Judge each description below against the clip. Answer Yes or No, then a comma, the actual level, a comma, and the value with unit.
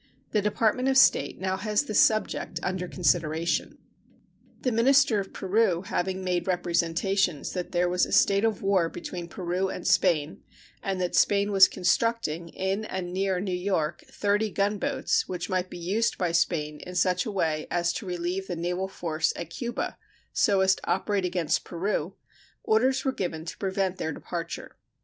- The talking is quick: No, average, 170 wpm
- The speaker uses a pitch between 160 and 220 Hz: Yes, medium, 185 Hz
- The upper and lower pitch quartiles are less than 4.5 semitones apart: Yes, narrow, 2.6 semitones